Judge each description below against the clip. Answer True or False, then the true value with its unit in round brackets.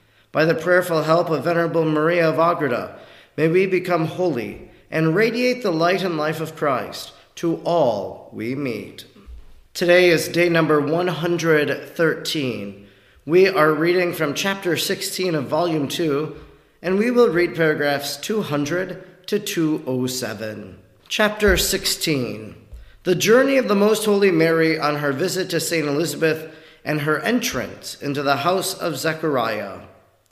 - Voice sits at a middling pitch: True (160 Hz)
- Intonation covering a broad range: False (3.8 semitones)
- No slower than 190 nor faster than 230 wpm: False (140 wpm)